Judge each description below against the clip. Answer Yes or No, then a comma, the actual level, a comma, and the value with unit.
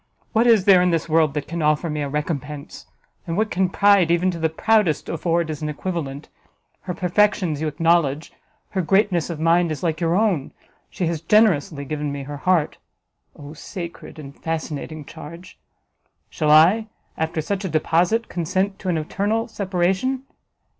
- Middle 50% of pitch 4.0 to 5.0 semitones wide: No, average, 3.5 semitones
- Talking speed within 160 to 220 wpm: Yes, average, 170 wpm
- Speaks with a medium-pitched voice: Yes, medium, 170 Hz